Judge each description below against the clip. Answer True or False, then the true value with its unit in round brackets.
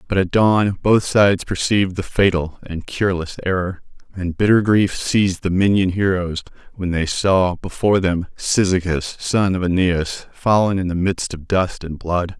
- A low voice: True (95 Hz)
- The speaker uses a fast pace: False (170 wpm)